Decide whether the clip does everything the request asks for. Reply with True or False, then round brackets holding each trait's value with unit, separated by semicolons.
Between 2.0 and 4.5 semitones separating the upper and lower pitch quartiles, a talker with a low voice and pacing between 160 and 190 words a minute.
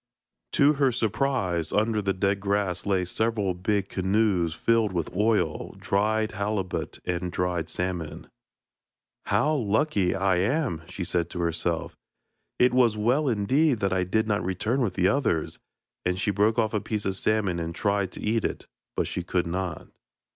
True (3.5 semitones; 100 Hz; 165 wpm)